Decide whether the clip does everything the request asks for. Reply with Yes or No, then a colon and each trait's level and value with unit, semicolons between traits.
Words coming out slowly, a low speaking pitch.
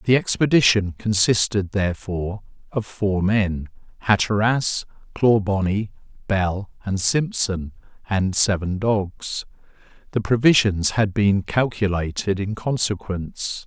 Yes: slow, 95 wpm; low, 100 Hz